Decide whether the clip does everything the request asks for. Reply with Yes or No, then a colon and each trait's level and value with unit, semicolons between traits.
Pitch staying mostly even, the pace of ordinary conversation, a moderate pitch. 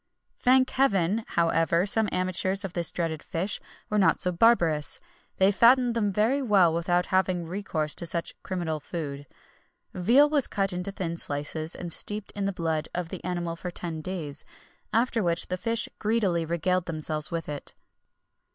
No: average, 3.7 semitones; average, 170 wpm; medium, 180 Hz